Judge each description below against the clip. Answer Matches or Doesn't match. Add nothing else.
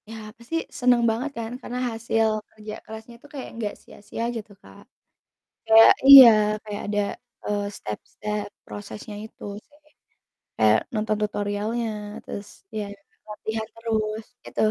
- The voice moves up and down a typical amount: Doesn't match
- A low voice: Doesn't match